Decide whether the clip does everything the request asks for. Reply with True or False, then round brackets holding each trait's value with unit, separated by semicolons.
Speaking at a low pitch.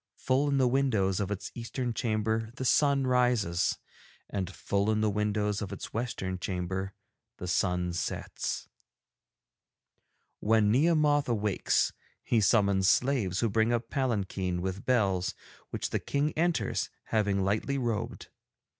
True (110 Hz)